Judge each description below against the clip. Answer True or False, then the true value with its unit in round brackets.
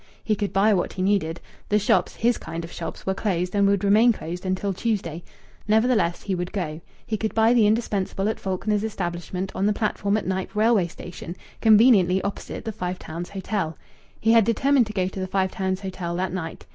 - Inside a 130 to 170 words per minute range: False (205 wpm)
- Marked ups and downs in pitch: False (3.0 semitones)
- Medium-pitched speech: False (195 Hz)